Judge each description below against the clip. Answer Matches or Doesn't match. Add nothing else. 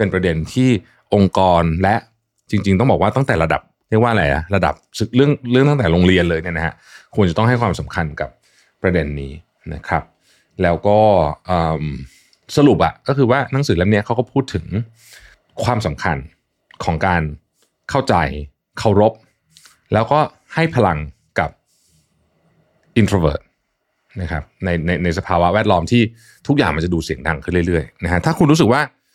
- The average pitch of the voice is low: Matches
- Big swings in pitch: Matches